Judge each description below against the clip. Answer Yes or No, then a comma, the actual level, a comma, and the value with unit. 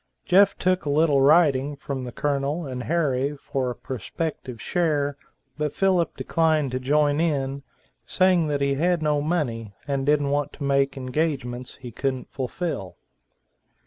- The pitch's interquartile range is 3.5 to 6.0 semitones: No, average, 3.0 semitones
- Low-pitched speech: No, medium, 145 Hz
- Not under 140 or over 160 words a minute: Yes, average, 150 wpm